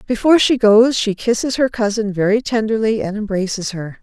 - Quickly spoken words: No, average, 180 wpm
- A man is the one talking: No, female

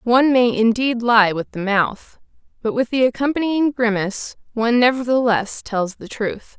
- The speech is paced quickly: No, average, 155 wpm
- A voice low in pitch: No, high, 235 Hz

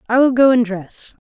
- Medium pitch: No, high, 235 Hz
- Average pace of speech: No, fast, 235 wpm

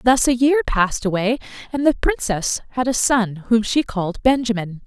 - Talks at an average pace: Yes, average, 185 wpm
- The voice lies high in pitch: Yes, high, 235 Hz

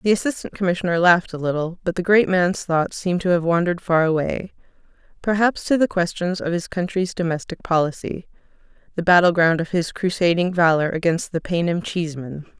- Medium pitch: Yes, medium, 175 Hz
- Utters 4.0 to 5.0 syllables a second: No, 5.7 syllables/s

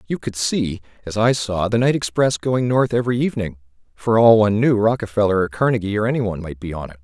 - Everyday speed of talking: No, fast, 220 wpm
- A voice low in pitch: Yes, low, 110 Hz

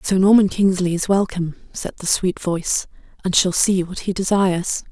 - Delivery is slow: No, average, 185 wpm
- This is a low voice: No, medium, 185 Hz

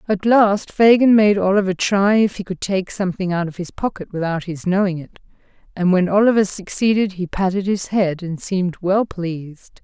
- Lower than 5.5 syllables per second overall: Yes, 5.1 syllables/s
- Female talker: Yes, female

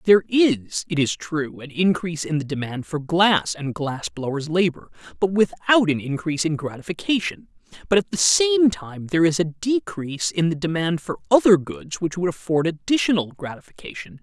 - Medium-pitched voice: Yes, medium, 165 Hz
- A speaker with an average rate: Yes, average, 175 wpm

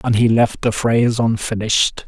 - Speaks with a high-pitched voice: No, low, 115 Hz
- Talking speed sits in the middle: Yes, average, 175 wpm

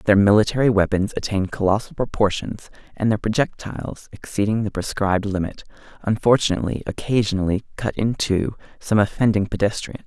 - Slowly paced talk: Yes, slow, 125 wpm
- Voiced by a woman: No, male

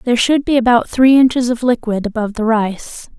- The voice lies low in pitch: No, high, 235 Hz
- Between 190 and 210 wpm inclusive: Yes, fast, 205 wpm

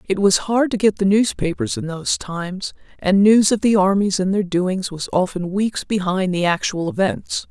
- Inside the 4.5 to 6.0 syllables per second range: Yes, 4.8 syllables/s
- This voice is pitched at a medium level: No, high, 195 Hz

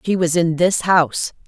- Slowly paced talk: No, fast, 205 wpm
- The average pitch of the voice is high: No, medium, 170 Hz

